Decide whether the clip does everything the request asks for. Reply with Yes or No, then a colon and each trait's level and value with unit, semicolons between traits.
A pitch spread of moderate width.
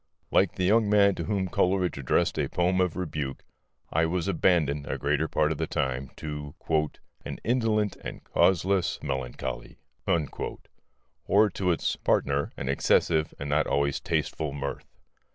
Yes: average, 4.8 semitones